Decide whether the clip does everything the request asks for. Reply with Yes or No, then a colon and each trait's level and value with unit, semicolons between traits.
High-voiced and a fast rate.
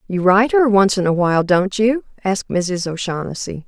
No: high, 195 Hz; average, 195 wpm